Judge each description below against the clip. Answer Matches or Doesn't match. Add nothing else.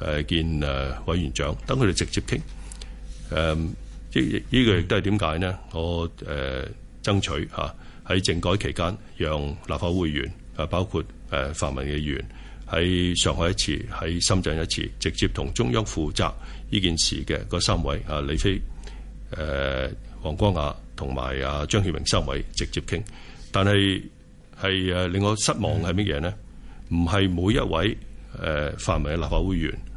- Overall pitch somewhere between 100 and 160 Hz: Doesn't match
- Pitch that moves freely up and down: Doesn't match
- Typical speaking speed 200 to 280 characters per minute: Matches